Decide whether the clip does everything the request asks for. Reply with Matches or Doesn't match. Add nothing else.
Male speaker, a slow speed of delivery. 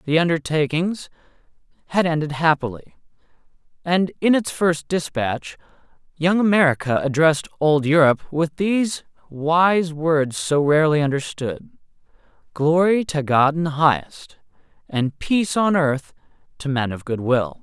Matches